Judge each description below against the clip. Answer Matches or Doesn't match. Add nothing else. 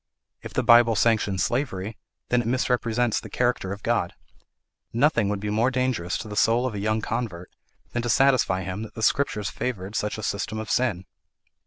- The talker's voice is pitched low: Matches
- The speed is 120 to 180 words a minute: Doesn't match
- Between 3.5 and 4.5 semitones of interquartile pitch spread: Doesn't match